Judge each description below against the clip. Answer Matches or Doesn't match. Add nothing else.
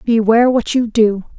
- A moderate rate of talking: Matches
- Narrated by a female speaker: Matches